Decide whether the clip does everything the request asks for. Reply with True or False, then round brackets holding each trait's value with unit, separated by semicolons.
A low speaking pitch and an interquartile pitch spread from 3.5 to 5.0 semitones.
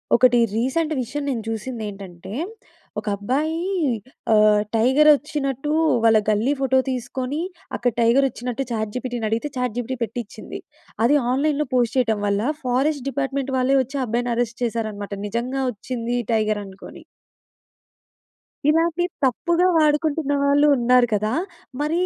False (250 Hz; 3.9 semitones)